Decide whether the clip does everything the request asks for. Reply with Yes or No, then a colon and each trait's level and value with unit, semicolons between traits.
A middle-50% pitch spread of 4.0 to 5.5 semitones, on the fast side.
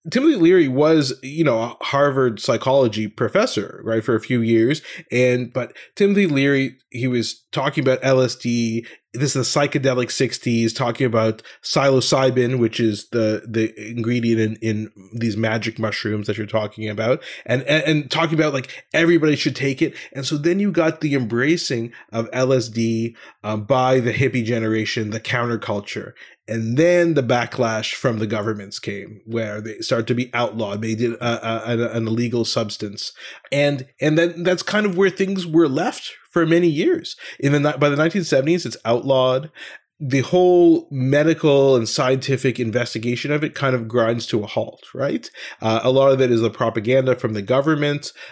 No: average, 4.3 semitones; average, 175 wpm